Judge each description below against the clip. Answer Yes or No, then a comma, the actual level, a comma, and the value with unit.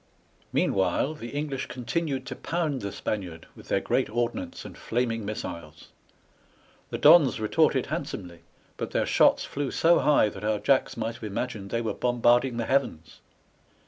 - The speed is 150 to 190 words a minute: Yes, average, 155 wpm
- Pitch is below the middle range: Yes, low, 120 Hz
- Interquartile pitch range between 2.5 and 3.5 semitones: No, average, 4.8 semitones